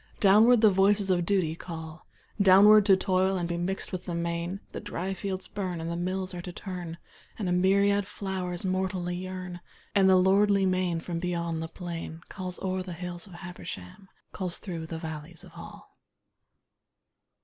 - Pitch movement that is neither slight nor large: No, narrow, 1.9 semitones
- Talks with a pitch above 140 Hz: Yes, medium, 185 Hz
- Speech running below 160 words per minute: No, average, 175 wpm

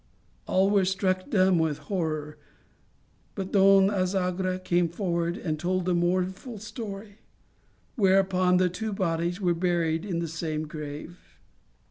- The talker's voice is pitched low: No, medium, 185 Hz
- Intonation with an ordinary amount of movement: No, narrow, 2.2 semitones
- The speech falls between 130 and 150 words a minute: Yes, slow, 135 wpm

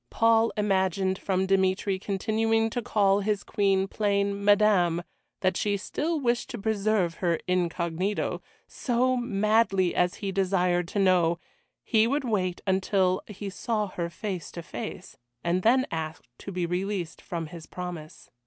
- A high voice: Yes, high, 195 Hz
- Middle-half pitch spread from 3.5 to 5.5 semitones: No, average, 3.0 semitones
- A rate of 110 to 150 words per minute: Yes, average, 145 wpm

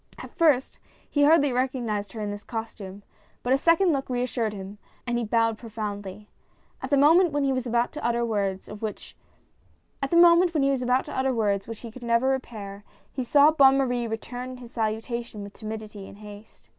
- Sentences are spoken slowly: No, average, 165 wpm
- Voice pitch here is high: Yes, high, 235 Hz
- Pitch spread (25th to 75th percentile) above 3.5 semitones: Yes, average, 4.0 semitones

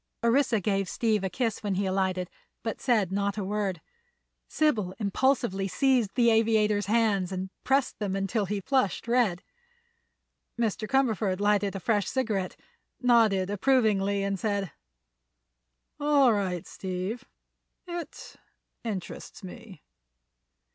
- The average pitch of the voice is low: No, high, 205 Hz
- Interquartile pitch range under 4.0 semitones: Yes, average, 3.4 semitones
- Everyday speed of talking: No, slow, 120 wpm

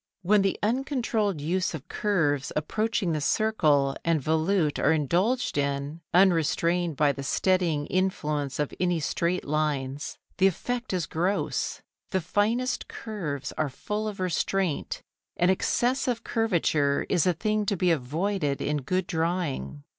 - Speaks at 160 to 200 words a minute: No, average, 140 wpm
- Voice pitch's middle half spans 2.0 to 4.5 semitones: No, average, 5.1 semitones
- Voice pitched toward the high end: No, medium, 175 Hz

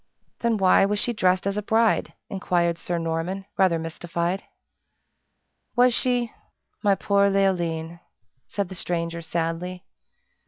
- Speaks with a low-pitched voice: No, medium, 185 Hz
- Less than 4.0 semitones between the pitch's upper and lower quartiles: Yes, average, 3.0 semitones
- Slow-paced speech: Yes, slow, 125 wpm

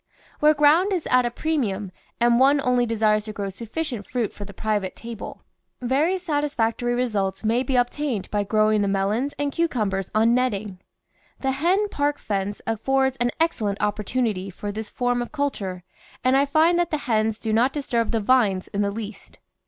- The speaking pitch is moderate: No, high, 235 Hz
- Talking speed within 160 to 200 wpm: Yes, average, 185 wpm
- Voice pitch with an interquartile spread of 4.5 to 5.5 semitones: Yes, average, 4.9 semitones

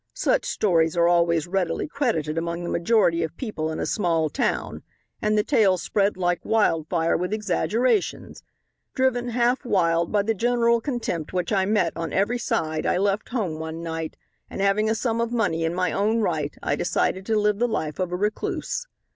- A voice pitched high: Yes, high, 195 Hz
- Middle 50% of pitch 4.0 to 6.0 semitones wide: Yes, average, 5.1 semitones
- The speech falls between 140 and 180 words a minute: No, average, 190 wpm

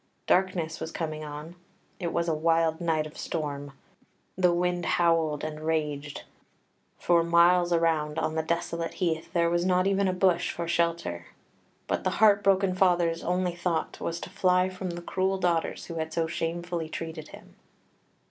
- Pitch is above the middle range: No, medium, 170 Hz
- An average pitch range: No, narrow, 1.9 semitones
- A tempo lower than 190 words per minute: Yes, average, 165 wpm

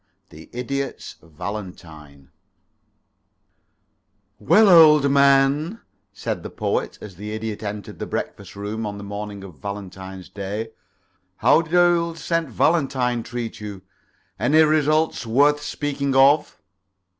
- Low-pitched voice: Yes, low, 115 Hz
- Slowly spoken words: Yes, slow, 120 wpm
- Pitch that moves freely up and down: Yes, wide, 6.6 semitones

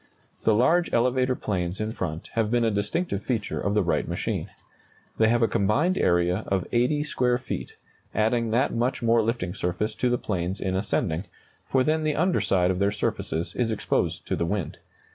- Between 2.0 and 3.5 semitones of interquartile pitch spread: No, average, 4.5 semitones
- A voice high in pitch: No, low, 110 Hz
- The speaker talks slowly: No, average, 190 wpm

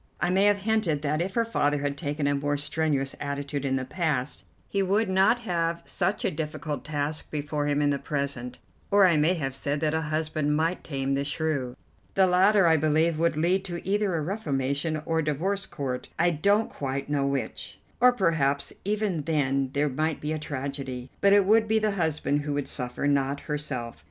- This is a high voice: No, medium, 150 Hz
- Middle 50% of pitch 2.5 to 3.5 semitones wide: No, average, 4.1 semitones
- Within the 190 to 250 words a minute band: Yes, average, 200 wpm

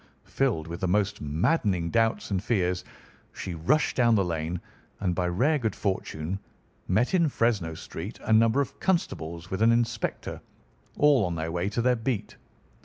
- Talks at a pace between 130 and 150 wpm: No, average, 170 wpm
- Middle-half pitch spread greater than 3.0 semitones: Yes, wide, 5.4 semitones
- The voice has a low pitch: Yes, low, 100 Hz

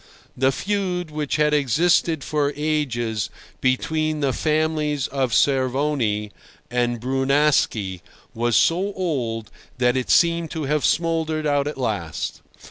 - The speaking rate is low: Yes, slow, 125 wpm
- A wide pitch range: No, average, 4.1 semitones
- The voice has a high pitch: No, medium, 145 Hz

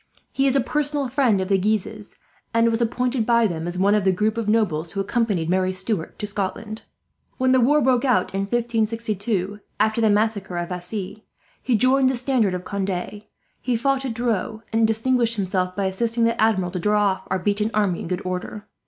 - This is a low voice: No, high, 215 Hz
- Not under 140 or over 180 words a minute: No, fast, 205 wpm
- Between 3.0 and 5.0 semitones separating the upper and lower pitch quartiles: Yes, average, 3.6 semitones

